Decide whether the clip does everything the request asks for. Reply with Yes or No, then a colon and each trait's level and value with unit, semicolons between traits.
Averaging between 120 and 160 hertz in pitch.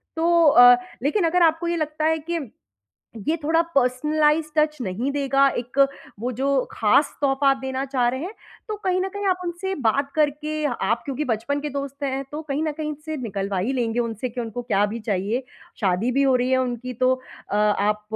No: very high, 275 Hz